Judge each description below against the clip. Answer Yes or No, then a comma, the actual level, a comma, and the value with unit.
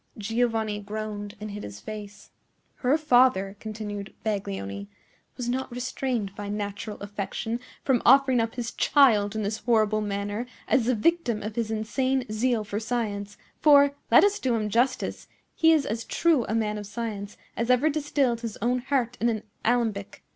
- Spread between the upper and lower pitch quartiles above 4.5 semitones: No, average, 3.3 semitones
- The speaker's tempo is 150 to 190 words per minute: Yes, average, 170 wpm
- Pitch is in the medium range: No, high, 225 Hz